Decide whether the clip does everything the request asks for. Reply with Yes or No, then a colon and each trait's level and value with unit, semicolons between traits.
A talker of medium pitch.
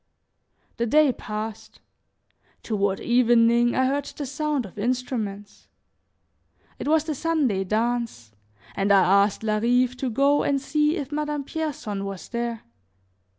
No: high, 240 Hz